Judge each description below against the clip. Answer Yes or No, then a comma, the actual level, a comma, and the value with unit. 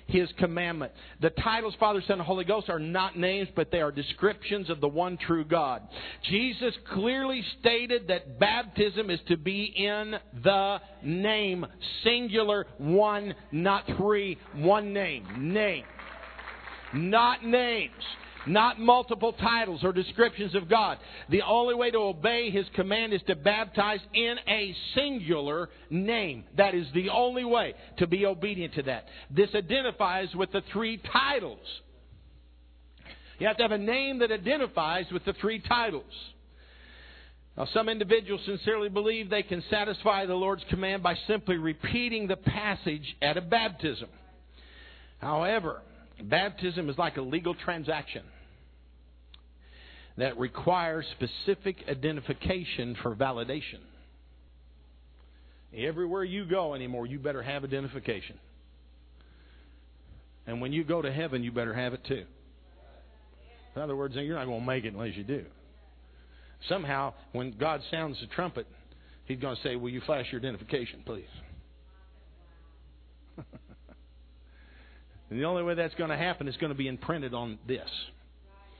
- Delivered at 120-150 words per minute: Yes, average, 140 wpm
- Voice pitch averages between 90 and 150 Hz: No, medium, 165 Hz